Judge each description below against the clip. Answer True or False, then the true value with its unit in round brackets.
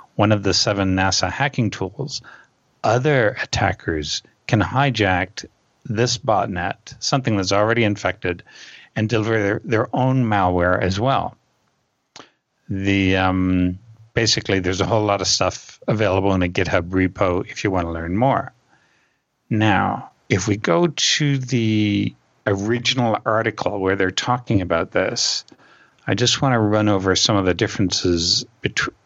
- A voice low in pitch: True (105 Hz)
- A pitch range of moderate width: True (3.9 semitones)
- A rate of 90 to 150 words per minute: True (140 wpm)